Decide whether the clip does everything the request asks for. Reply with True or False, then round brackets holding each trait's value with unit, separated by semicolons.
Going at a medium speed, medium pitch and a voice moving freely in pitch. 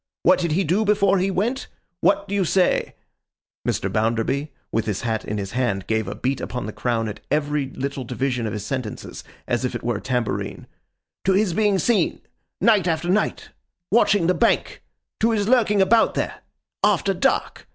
True (170 wpm; 150 Hz; 9.0 semitones)